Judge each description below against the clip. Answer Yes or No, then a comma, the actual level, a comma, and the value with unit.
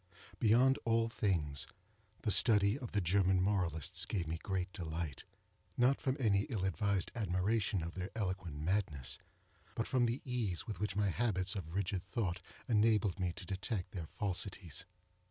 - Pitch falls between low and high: No, low, 100 Hz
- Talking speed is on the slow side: No, average, 155 wpm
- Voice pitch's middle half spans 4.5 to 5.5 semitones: No, average, 3.5 semitones